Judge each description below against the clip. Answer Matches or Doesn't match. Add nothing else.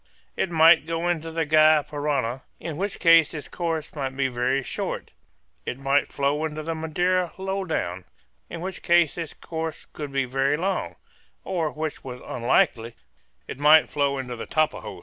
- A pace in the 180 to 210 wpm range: Doesn't match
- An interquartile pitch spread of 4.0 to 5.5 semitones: Doesn't match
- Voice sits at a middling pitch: Matches